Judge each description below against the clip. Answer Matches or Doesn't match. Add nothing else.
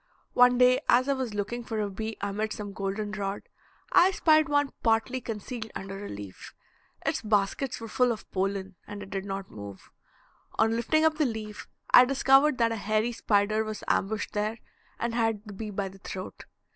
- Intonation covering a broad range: Doesn't match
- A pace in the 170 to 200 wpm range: Matches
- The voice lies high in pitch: Matches